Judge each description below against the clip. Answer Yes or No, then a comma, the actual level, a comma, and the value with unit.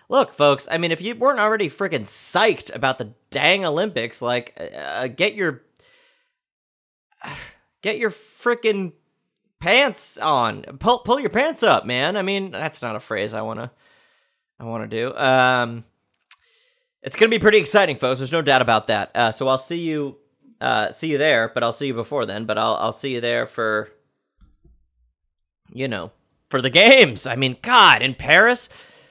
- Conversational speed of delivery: Yes, average, 175 wpm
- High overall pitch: No, medium, 140 Hz